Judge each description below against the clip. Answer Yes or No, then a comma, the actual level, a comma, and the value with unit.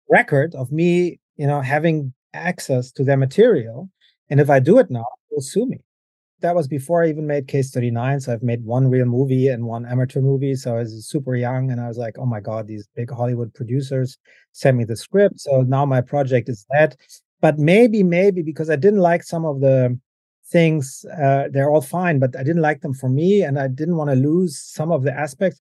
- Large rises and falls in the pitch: No, average, 4.0 semitones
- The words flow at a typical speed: No, fast, 220 wpm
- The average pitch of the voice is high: No, medium, 140 Hz